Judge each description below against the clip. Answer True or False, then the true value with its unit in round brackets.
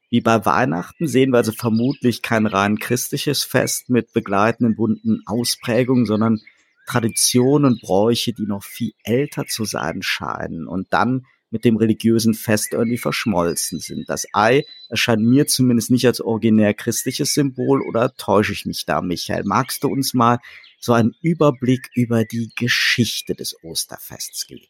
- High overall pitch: False (120 Hz)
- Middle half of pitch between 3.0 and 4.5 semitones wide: False (2.4 semitones)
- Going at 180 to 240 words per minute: False (155 wpm)